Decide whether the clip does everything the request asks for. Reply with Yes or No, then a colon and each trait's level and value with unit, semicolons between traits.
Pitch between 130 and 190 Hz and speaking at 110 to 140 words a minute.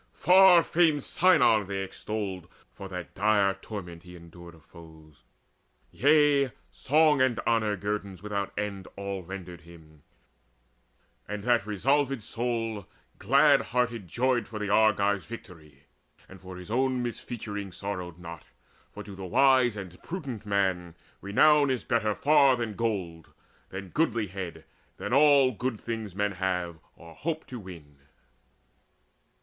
No: low, 105 Hz; slow, 135 wpm